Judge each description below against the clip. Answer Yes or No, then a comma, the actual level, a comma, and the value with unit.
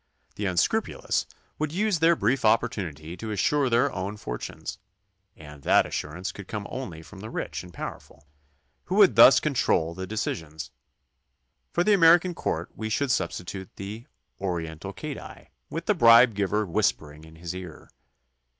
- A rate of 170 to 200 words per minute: No, average, 160 wpm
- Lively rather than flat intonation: Yes, wide, 6.9 semitones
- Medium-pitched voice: No, low, 100 Hz